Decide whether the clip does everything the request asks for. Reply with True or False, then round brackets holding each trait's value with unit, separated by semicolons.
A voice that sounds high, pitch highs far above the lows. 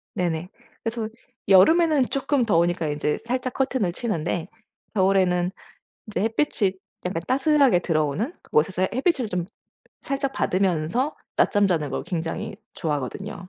True (195 Hz; 6.7 semitones)